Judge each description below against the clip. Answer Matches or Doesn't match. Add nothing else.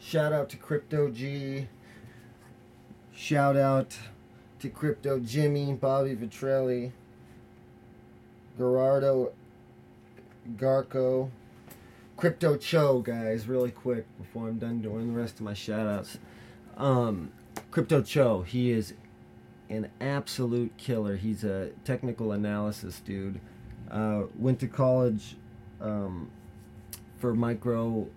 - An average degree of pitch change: Matches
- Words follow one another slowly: Matches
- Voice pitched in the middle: Doesn't match